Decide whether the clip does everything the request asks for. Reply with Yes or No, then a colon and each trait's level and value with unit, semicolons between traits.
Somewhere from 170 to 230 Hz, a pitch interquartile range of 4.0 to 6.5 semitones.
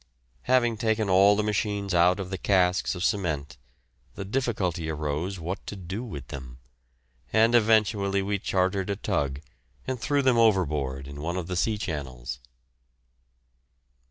No: very low, 95 Hz; average, 4.6 semitones